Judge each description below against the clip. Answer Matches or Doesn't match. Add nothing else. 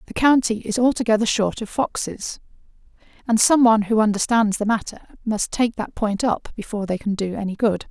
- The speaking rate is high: Doesn't match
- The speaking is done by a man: Doesn't match